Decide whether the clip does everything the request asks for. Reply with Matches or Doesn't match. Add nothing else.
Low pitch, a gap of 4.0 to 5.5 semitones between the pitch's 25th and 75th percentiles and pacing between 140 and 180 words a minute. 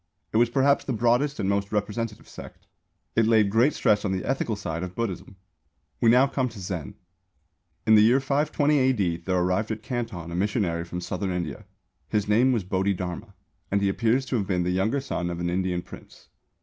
Doesn't match